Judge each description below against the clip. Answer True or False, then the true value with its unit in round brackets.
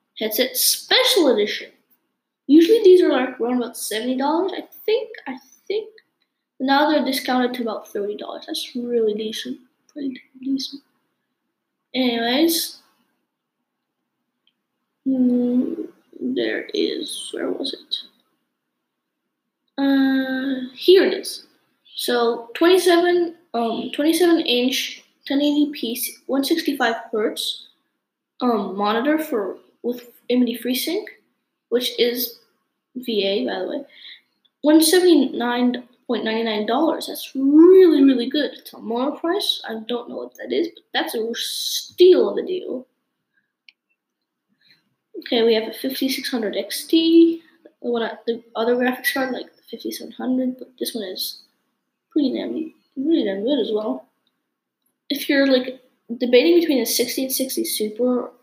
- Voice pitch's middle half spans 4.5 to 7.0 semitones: True (4.9 semitones)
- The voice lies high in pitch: True (270 Hz)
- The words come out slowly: True (125 wpm)